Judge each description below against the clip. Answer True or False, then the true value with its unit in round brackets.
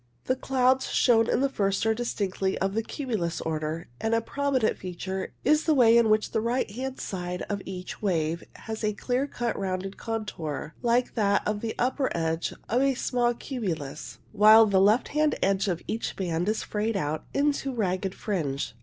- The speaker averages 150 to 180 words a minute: False (190 wpm)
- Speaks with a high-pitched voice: True (215 Hz)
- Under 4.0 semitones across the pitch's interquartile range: False (4.7 semitones)